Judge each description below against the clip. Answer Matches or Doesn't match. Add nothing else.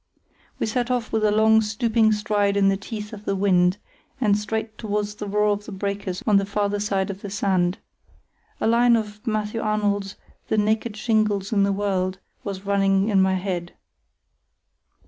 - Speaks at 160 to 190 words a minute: Matches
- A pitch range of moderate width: Doesn't match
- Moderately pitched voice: Doesn't match